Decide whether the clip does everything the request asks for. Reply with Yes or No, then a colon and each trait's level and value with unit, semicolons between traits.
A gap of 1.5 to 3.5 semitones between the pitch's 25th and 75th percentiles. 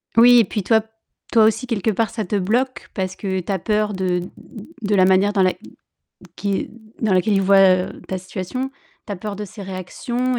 Yes: average, 2.9 semitones